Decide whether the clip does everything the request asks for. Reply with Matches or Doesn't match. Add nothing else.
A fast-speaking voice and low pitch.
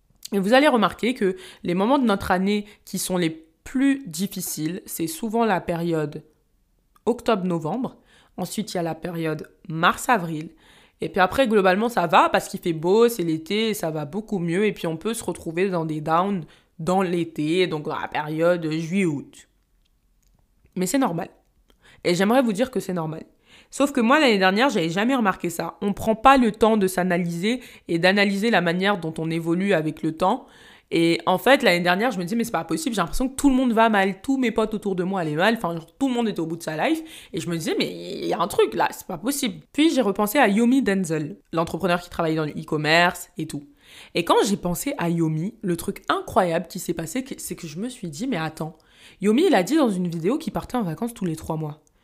Doesn't match